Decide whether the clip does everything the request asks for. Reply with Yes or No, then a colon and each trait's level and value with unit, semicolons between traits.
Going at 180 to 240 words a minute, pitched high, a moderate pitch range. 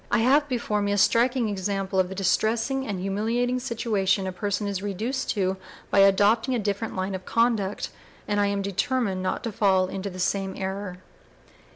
Yes: average, 185 wpm; high, 200 Hz; average, 3.2 semitones